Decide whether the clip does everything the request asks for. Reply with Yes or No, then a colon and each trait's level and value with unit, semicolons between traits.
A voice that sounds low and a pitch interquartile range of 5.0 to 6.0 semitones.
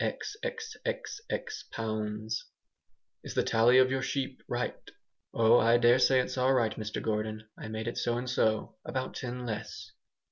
No: low, 120 Hz; average, 3.0 semitones